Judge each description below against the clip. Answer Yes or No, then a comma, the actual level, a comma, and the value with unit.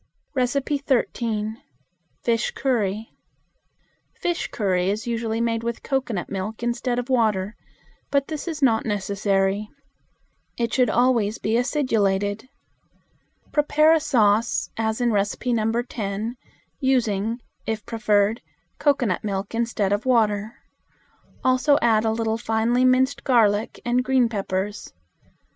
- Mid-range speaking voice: No, high, 230 Hz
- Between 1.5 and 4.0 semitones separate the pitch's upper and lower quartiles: Yes, average, 3.3 semitones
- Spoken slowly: Yes, slow, 115 wpm